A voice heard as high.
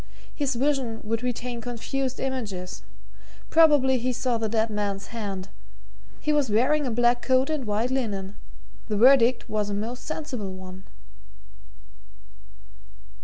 Yes: high, 240 Hz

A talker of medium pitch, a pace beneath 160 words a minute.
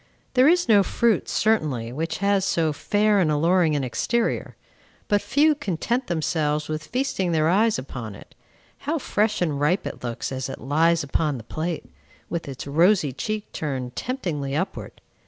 No: medium, 165 Hz; average, 165 wpm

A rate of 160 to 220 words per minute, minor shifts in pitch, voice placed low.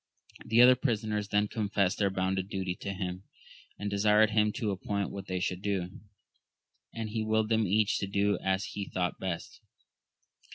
Yes: average, 170 wpm; narrow, 2.1 semitones; low, 100 Hz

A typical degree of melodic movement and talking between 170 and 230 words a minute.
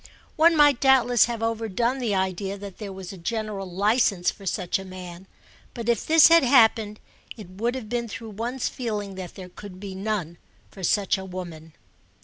Yes: average, 3.9 semitones; average, 185 wpm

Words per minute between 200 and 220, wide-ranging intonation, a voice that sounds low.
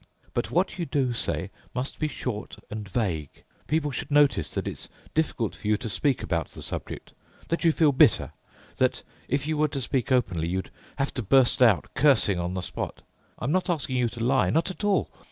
Yes: fast, 205 wpm; wide, 6.0 semitones; low, 130 Hz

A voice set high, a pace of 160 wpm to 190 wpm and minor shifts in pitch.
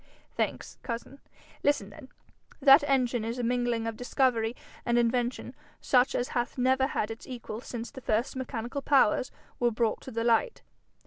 Yes: high, 245 Hz; average, 165 wpm; narrow, 2.2 semitones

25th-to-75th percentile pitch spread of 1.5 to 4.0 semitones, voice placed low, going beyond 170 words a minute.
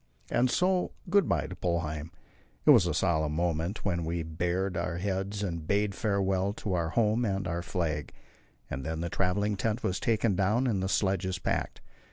Yes: average, 3.1 semitones; very low, 95 Hz; average, 185 wpm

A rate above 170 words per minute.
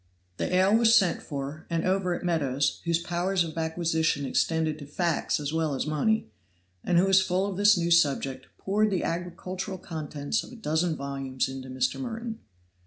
Yes: average, 180 wpm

